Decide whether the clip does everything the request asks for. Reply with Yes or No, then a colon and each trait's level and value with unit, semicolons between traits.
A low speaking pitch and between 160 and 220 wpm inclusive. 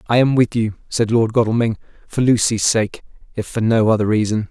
Yes: low, 110 Hz; average, 200 wpm